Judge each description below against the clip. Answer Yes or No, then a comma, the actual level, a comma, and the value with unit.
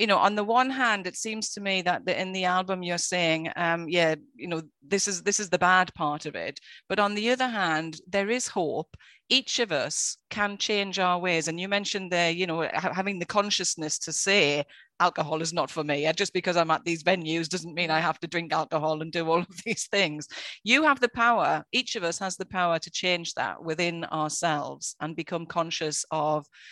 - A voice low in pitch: No, medium, 180 Hz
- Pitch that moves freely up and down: No, average, 3.6 semitones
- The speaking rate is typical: No, fast, 220 wpm